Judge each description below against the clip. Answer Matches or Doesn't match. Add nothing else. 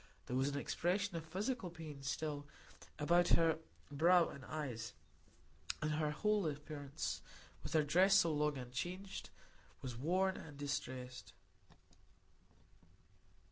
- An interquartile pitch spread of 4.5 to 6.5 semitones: Doesn't match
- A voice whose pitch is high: Doesn't match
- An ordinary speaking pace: Doesn't match